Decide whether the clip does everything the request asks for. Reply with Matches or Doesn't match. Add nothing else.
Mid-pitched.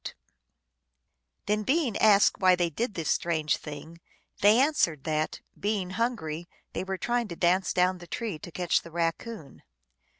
Matches